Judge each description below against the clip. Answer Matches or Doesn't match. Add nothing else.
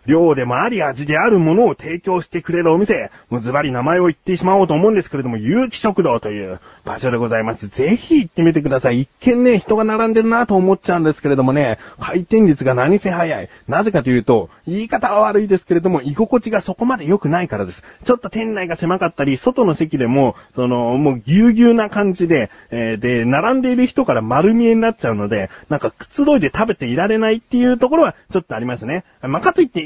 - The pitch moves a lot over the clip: Matches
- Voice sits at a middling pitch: Matches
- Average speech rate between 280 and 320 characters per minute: Doesn't match